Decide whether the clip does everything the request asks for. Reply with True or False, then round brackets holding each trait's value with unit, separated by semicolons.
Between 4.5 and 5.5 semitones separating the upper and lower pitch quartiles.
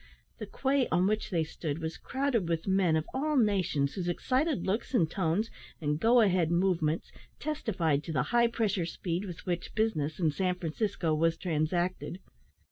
True (5.2 semitones)